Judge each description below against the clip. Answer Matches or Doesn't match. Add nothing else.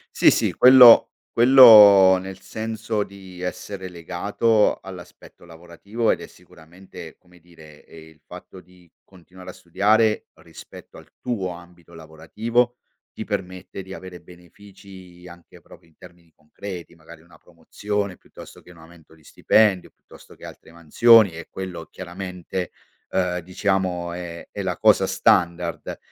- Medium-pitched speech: Doesn't match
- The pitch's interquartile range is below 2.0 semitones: Doesn't match